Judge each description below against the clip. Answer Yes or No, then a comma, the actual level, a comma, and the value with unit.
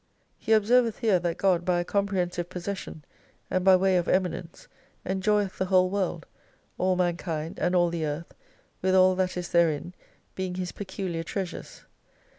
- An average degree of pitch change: No, narrow, 1.7 semitones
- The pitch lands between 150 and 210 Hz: Yes, medium, 185 Hz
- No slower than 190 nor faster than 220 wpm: No, average, 160 wpm